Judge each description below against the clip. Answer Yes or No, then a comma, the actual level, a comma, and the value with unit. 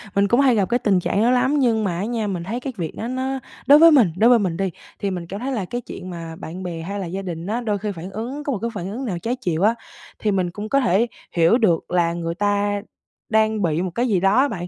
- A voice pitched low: No, high, 205 Hz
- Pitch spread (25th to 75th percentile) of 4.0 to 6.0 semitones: Yes, average, 5.0 semitones